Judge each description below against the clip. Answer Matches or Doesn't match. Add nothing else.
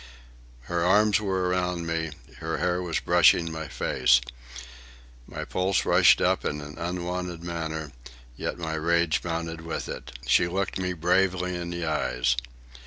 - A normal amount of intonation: Doesn't match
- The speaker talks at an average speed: Matches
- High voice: Doesn't match